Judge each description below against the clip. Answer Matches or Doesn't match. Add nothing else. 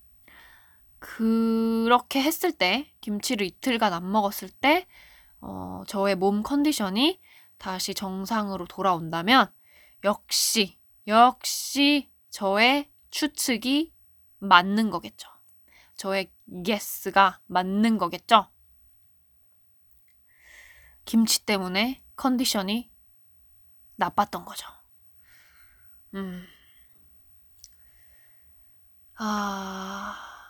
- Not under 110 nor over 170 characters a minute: Matches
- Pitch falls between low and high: Doesn't match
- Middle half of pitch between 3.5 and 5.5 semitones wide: Matches